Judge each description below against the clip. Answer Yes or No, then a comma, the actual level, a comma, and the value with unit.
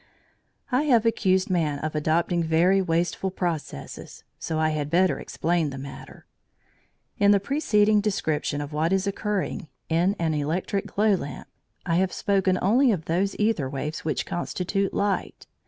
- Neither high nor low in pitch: Yes, medium, 180 Hz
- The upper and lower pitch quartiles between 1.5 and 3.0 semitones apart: No, average, 4.1 semitones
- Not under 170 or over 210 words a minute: No, average, 155 wpm